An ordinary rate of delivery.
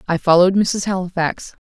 Yes: average, 145 wpm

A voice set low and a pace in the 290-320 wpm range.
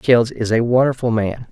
No: low, 120 Hz; average, 200 wpm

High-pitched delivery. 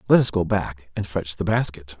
No: very low, 90 Hz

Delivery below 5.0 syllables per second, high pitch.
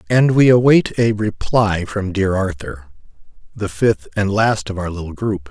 No: 4.3 syllables/s; low, 100 Hz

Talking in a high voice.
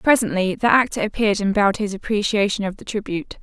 Yes: high, 205 Hz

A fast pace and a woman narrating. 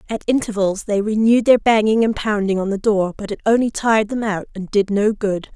Yes: fast, 225 wpm; female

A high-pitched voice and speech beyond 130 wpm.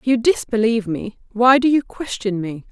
Yes: high, 230 Hz; average, 200 wpm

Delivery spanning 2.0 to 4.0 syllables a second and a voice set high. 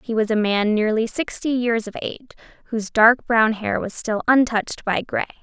No: 5.4 syllables/s; high, 225 Hz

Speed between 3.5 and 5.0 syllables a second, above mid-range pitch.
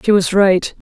Yes: 4.4 syllables/s; high, 195 Hz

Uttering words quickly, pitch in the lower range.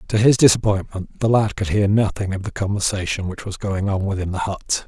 Yes: fast, 220 wpm; low, 100 Hz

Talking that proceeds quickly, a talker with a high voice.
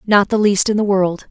Yes: fast, 275 wpm; high, 200 Hz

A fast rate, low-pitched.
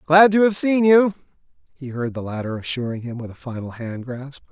No: fast, 215 wpm; medium, 145 Hz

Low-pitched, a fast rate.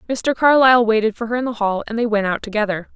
No: high, 225 Hz; fast, 265 wpm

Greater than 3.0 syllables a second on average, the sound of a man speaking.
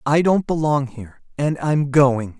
Yes: 4.3 syllables/s; male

